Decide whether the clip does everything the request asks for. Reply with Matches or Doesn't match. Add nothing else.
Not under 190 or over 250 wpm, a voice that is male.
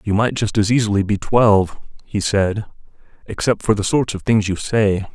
Matches